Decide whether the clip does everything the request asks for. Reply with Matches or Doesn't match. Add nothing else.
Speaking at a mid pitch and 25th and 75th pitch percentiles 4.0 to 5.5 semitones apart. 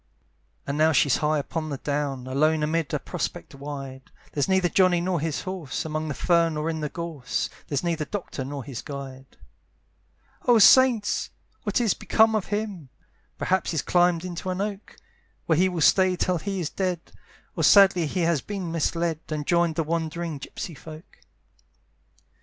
Doesn't match